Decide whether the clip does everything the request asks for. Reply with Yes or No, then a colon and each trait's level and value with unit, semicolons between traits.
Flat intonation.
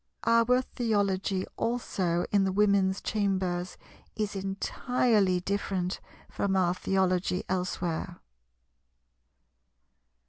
Yes: narrow, 2.1 semitones